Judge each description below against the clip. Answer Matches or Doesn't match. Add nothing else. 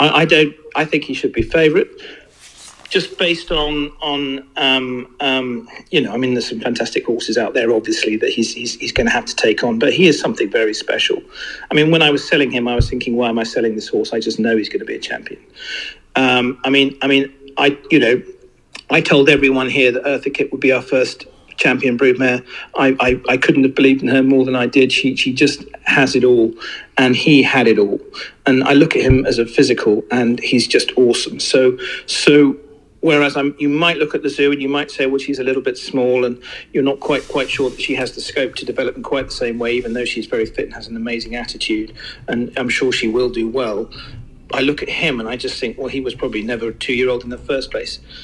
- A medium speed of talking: Doesn't match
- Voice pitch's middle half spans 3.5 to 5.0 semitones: Doesn't match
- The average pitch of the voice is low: Matches